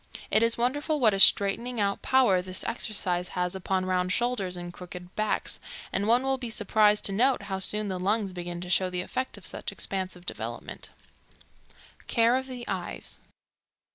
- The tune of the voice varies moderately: Yes, average, 4.4 semitones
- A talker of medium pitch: No, high, 200 Hz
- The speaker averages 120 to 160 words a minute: No, average, 175 wpm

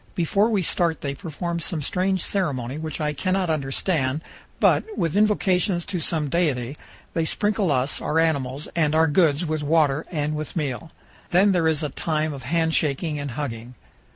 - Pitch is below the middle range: No, medium, 160 Hz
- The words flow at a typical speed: Yes, average, 170 wpm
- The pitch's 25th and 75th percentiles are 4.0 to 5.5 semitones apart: No, average, 3.3 semitones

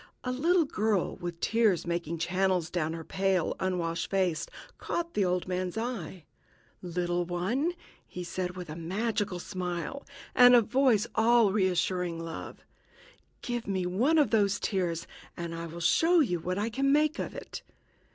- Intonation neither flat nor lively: Yes, average, 4.9 semitones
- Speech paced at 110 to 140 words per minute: No, average, 160 wpm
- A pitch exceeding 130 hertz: Yes, medium, 185 Hz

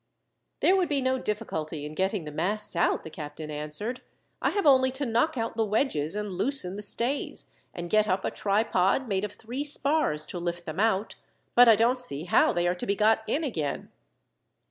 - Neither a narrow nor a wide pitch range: No, wide, 6.3 semitones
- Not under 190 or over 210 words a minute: Yes, fast, 205 wpm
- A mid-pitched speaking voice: No, high, 210 Hz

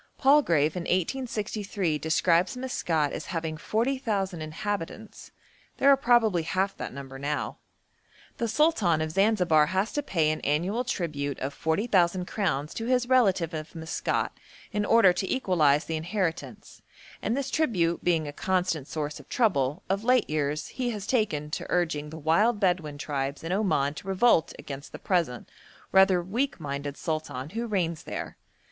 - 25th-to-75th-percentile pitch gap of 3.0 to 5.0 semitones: No, wide, 5.6 semitones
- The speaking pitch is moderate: Yes, medium, 175 Hz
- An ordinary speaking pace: Yes, average, 155 wpm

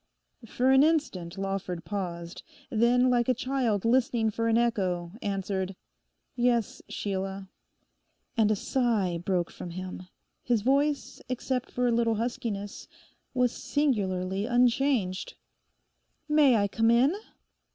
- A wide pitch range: No, average, 4.5 semitones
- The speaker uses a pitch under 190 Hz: No, high, 225 Hz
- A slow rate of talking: Yes, slow, 120 wpm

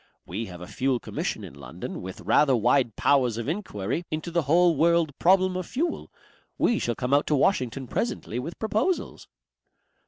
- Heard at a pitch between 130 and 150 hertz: Yes, medium, 140 Hz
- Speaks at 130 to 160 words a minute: No, average, 175 wpm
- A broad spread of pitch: Yes, wide, 6.7 semitones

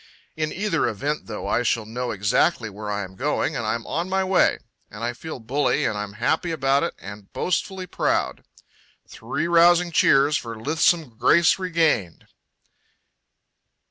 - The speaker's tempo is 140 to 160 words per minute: Yes, average, 155 wpm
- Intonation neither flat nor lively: No, wide, 7.4 semitones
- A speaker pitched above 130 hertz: Yes, medium, 140 Hz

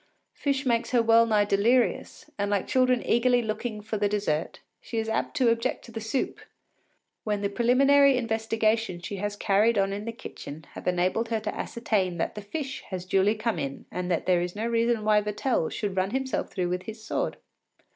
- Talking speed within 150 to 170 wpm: No, average, 200 wpm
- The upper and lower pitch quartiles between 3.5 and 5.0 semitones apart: No, average, 2.9 semitones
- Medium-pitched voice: No, high, 220 Hz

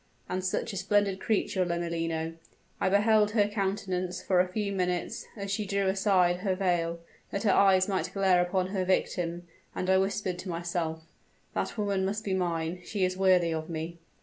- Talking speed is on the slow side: No, average, 180 wpm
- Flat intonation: Yes, narrow, 2.1 semitones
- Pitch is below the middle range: No, medium, 185 Hz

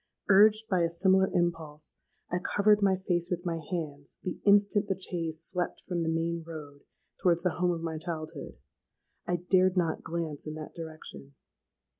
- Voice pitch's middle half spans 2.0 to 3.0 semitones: Yes, narrow, 2.6 semitones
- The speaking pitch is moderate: Yes, medium, 170 Hz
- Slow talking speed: No, average, 170 wpm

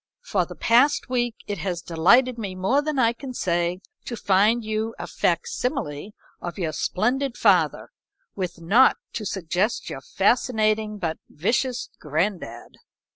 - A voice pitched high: Yes, high, 210 Hz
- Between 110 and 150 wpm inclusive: Yes, average, 145 wpm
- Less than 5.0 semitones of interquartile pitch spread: No, wide, 5.5 semitones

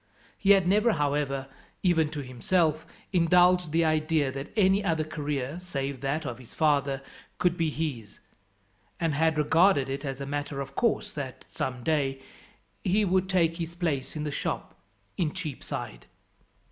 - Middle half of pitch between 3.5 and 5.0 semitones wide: Yes, average, 4.1 semitones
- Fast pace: No, average, 160 wpm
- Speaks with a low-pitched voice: No, medium, 155 Hz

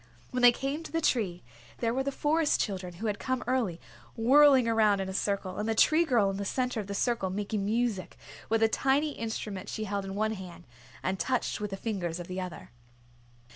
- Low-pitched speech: No, high, 220 Hz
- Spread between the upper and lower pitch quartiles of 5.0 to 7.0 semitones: No, average, 4.5 semitones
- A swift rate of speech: Yes, fast, 215 wpm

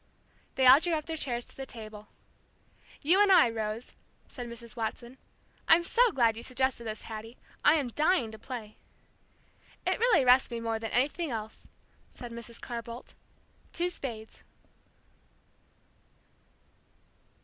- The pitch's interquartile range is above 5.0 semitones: No, average, 4.1 semitones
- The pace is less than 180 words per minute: Yes, average, 145 wpm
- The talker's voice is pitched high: Yes, high, 240 Hz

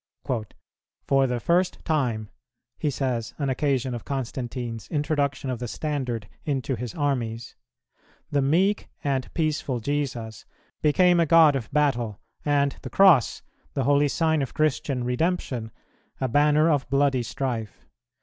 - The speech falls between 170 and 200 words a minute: No, slow, 135 wpm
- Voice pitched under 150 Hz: Yes, low, 135 Hz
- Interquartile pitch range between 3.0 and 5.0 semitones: Yes, average, 3.4 semitones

